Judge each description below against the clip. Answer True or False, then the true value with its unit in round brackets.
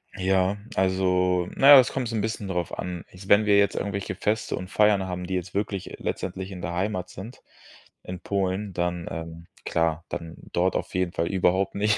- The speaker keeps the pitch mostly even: True (2.2 semitones)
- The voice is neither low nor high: False (95 Hz)